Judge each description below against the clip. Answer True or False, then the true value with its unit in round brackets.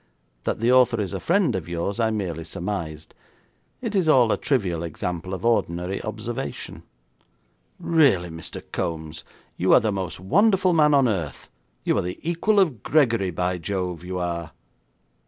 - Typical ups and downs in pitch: False (6.8 semitones)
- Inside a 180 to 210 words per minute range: False (160 wpm)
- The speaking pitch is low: True (100 Hz)